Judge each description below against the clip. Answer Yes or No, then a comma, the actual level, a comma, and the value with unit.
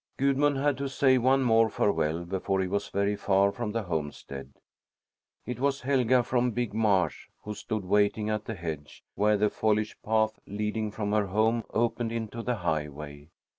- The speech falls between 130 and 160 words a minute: No, average, 170 wpm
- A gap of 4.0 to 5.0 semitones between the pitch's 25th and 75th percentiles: No, average, 3.5 semitones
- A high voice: No, low, 105 Hz